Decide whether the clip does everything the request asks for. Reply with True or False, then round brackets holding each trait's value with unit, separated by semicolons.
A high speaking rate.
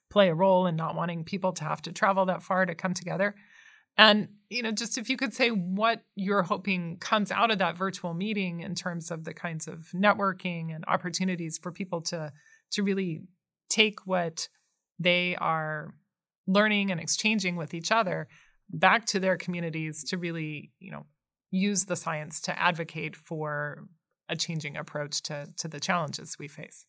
False (180 wpm)